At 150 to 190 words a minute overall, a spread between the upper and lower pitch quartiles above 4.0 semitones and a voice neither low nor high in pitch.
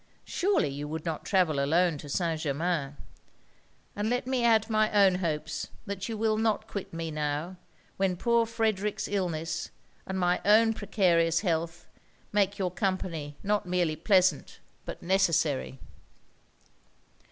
No: average, 140 wpm; average, 4.5 semitones; medium, 180 Hz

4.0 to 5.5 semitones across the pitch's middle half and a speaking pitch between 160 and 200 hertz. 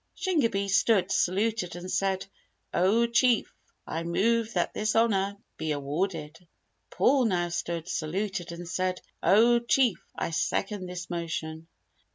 Yes: average, 4.7 semitones; high, 190 Hz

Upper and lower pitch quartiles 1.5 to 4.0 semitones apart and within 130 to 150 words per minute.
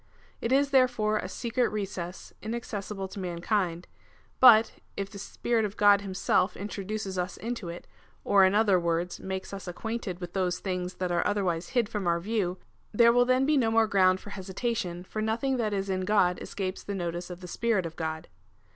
No: average, 3.5 semitones; average, 190 wpm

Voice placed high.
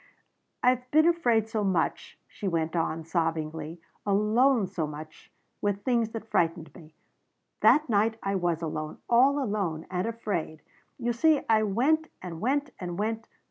Yes: high, 205 Hz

